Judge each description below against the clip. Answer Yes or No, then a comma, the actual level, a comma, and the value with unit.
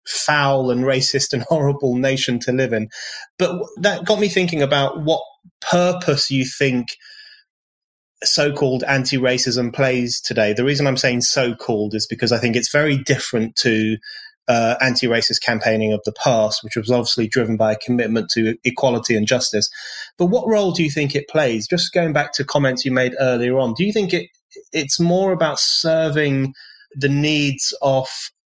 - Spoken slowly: No, average, 170 wpm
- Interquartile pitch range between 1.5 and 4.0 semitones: No, average, 4.8 semitones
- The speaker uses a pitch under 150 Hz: Yes, low, 135 Hz